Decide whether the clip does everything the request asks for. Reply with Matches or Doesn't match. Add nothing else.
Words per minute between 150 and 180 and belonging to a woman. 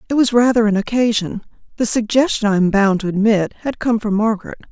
Doesn't match